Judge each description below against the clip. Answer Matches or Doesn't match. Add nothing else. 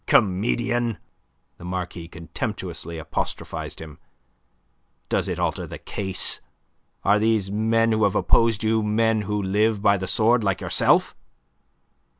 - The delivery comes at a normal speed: Doesn't match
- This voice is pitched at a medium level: Doesn't match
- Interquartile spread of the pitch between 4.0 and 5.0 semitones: Doesn't match